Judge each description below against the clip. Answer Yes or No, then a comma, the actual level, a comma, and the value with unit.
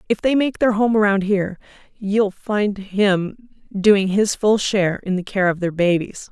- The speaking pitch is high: Yes, high, 200 Hz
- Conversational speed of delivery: Yes, average, 190 wpm